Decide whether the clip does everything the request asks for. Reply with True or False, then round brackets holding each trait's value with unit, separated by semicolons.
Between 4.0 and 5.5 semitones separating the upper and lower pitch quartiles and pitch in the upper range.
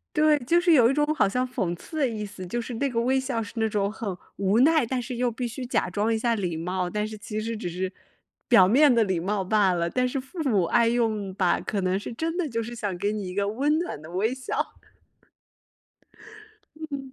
True (4.6 semitones; 225 Hz)